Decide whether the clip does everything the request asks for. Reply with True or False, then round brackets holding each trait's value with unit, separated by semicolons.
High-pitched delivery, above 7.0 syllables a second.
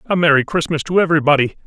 False (155 Hz; 7.5 syllables/s)